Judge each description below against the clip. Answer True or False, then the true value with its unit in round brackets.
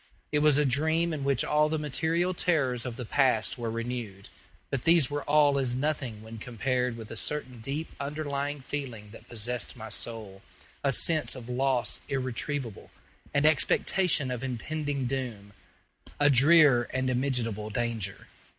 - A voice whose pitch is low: True (130 Hz)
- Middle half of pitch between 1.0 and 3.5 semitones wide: False (3.9 semitones)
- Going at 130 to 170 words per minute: True (155 wpm)